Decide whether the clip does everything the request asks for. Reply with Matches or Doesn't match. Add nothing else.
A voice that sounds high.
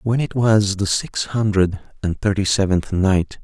Doesn't match